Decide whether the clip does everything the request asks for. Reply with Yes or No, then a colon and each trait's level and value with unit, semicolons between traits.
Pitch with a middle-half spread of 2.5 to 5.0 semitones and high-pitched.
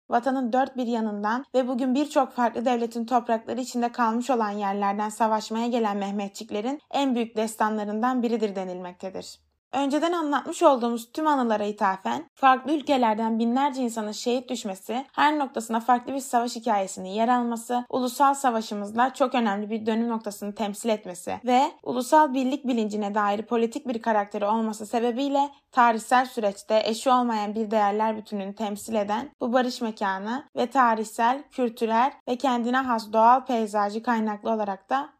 Yes: average, 3.2 semitones; high, 235 Hz